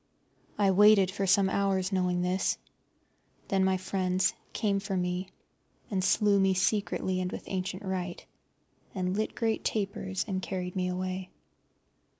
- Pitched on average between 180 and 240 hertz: Yes, high, 190 Hz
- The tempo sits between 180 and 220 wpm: No, average, 145 wpm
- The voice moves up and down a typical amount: No, narrow, 1.2 semitones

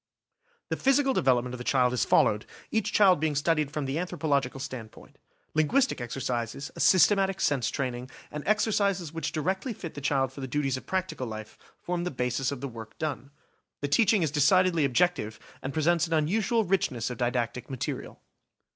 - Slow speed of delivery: No, average, 180 wpm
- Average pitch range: No, wide, 6.0 semitones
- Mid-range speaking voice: Yes, medium, 145 Hz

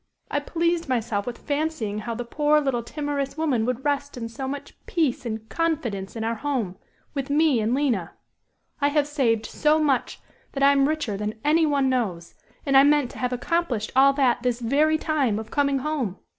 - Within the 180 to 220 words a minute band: Yes, average, 195 wpm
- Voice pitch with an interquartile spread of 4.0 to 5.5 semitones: Yes, average, 4.3 semitones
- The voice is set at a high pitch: Yes, very high, 270 Hz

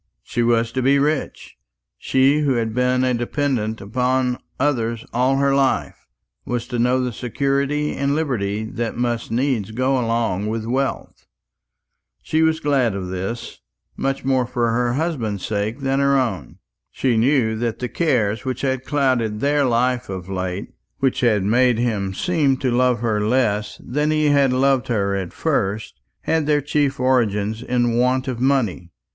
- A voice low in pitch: Yes, low, 125 Hz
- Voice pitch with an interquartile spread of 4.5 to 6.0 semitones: No, average, 3.5 semitones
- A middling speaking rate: Yes, average, 165 wpm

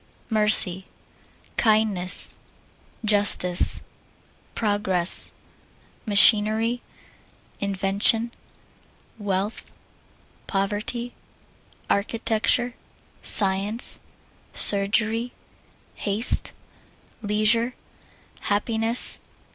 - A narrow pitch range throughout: Yes, narrow, 2.3 semitones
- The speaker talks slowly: Yes, slow, 45 wpm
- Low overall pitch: No, high, 210 Hz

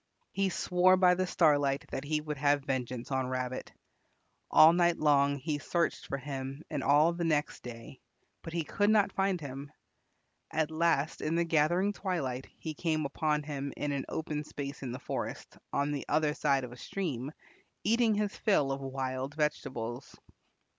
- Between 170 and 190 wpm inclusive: Yes, average, 175 wpm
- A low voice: No, medium, 150 Hz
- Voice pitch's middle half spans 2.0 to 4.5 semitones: Yes, average, 3.6 semitones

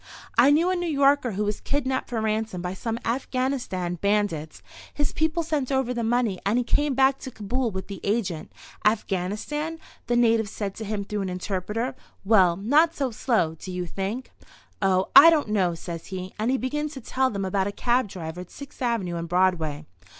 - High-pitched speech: Yes, high, 220 Hz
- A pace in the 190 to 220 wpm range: Yes, average, 195 wpm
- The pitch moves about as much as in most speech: No, wide, 5.7 semitones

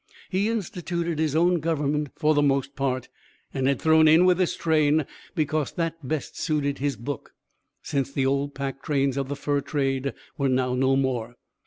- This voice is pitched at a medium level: Yes, medium, 145 Hz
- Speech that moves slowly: No, average, 180 wpm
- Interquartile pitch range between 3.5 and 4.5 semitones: No, average, 2.7 semitones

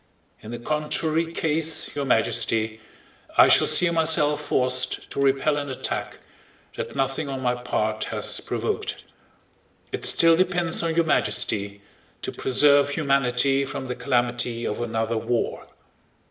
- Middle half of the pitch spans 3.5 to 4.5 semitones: Yes, average, 4.0 semitones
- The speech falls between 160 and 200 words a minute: No, slow, 135 wpm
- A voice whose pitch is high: No, low, 135 Hz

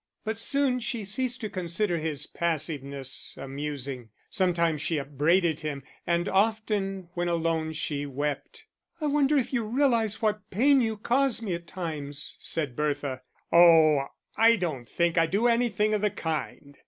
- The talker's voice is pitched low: No, medium, 170 Hz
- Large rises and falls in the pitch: Yes, wide, 6.5 semitones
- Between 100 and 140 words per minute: No, average, 155 wpm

